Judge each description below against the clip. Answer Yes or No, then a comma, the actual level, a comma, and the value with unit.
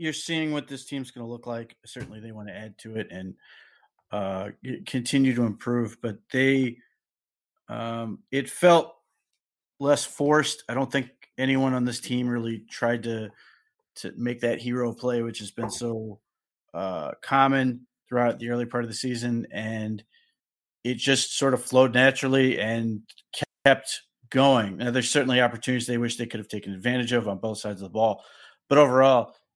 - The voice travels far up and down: No, average, 2.8 semitones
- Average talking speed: Yes, average, 175 wpm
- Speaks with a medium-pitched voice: No, low, 120 Hz